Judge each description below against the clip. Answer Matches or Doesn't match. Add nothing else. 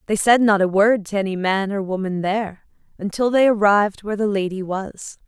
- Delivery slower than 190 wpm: Doesn't match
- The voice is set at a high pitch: Matches